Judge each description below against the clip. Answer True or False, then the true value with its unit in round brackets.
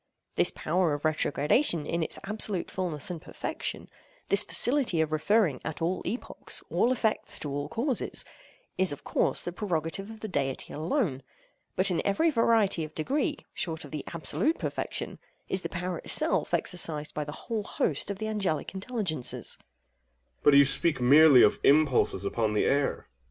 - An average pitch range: False (6.0 semitones)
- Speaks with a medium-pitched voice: True (170 Hz)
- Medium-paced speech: True (160 wpm)